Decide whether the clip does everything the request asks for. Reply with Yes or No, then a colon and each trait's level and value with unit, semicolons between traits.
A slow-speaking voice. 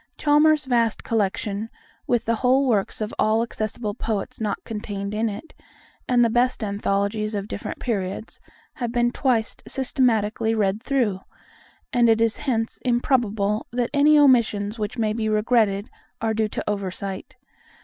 No: average, 150 wpm